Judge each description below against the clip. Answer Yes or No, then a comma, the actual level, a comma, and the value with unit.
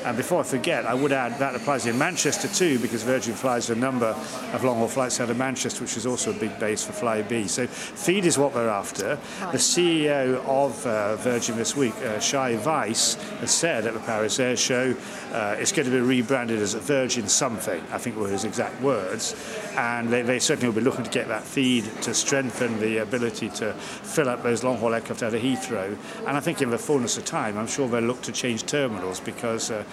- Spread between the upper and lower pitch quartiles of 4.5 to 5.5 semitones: No, narrow, 2.5 semitones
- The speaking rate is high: Yes, fast, 225 wpm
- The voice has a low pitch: Yes, low, 125 Hz